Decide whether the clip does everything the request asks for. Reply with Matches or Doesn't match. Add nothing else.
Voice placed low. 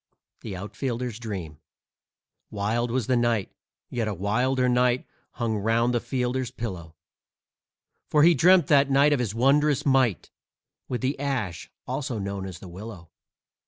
Matches